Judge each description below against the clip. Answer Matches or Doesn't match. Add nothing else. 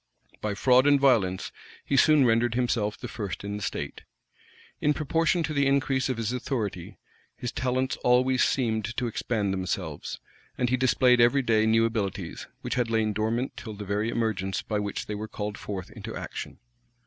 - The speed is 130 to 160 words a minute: Doesn't match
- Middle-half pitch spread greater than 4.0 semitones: Doesn't match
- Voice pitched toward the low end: Matches